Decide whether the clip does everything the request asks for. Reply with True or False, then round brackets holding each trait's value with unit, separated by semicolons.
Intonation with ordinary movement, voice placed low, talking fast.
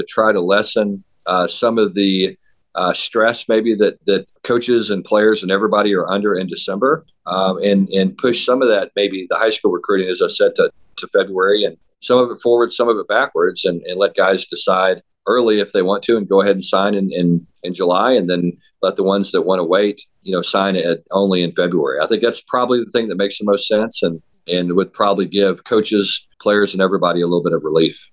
True (3.6 semitones; 100 Hz; 235 wpm)